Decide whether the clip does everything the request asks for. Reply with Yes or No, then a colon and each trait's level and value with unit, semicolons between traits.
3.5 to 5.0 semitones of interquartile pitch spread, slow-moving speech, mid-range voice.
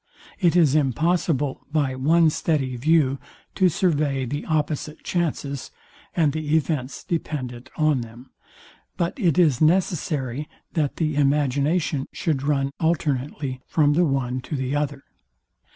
No: average, 3.0 semitones; slow, 130 wpm; medium, 145 Hz